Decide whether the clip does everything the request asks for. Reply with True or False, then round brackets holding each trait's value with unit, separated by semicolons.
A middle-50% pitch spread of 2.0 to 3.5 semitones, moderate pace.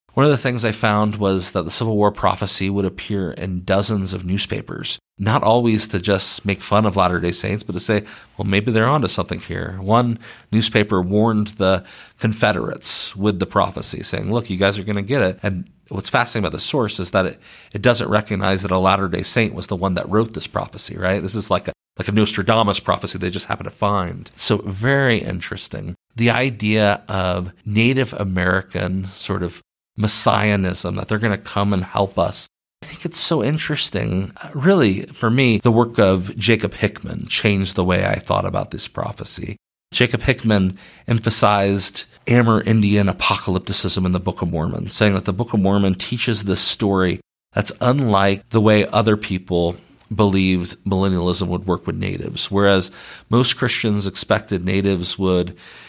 True (2.8 semitones; 185 wpm)